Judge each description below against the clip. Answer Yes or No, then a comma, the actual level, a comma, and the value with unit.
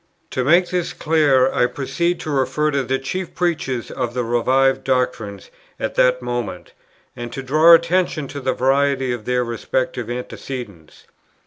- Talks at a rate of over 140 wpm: Yes, average, 155 wpm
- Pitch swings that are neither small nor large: Yes, average, 3.5 semitones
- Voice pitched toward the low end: Yes, low, 130 Hz